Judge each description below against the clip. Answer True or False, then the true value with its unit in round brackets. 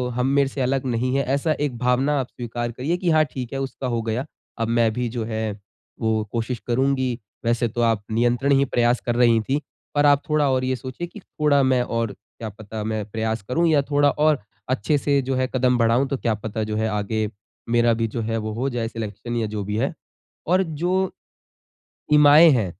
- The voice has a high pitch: False (125 Hz)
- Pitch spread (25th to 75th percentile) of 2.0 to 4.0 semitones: True (3.5 semitones)